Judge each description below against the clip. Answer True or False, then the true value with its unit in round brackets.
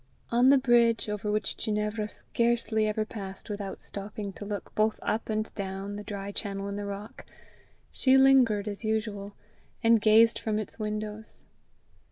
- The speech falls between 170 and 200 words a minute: False (160 wpm)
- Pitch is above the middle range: True (215 Hz)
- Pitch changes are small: True (1.7 semitones)